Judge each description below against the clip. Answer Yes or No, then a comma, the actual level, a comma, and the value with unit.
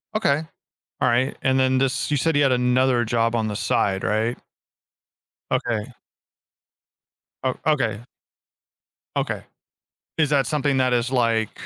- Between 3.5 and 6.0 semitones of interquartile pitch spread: No, narrow, 2.6 semitones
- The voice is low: Yes, low, 125 Hz